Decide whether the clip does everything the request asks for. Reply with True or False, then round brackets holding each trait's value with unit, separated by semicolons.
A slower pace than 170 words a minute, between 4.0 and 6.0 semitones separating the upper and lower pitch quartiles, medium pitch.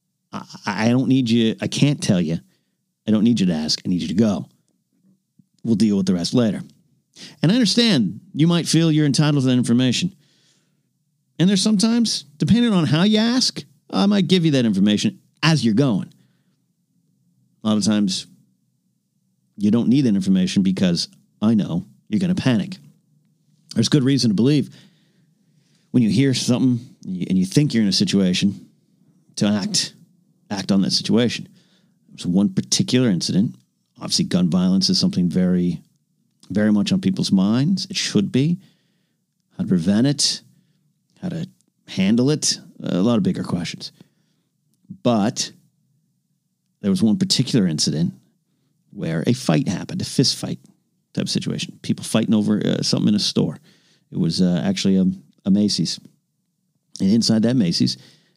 True (160 wpm; 4.4 semitones; 180 Hz)